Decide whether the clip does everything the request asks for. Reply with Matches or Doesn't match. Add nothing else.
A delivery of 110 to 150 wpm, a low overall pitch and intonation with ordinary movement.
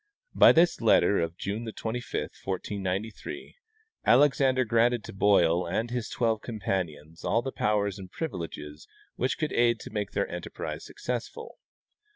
Matches